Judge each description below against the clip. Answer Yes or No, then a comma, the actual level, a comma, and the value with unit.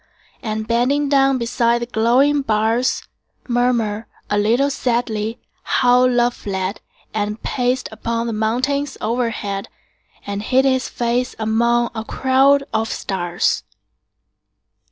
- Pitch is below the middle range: No, high, 235 Hz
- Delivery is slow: Yes, slow, 120 wpm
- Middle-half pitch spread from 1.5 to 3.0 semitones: Yes, average, 2.7 semitones